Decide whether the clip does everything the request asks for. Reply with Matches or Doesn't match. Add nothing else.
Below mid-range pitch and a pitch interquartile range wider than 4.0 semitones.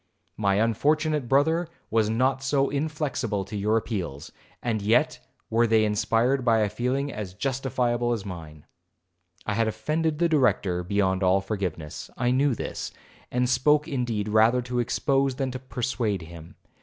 Matches